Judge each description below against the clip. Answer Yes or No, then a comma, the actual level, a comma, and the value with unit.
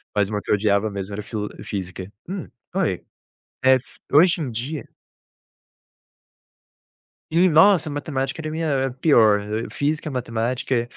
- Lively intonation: Yes, wide, 6.7 semitones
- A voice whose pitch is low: Yes, low, 130 Hz